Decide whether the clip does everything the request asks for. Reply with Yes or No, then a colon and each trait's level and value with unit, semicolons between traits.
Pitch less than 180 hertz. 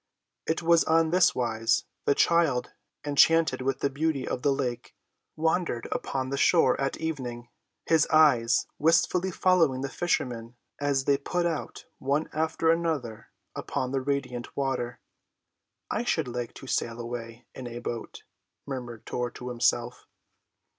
Yes: low, 135 Hz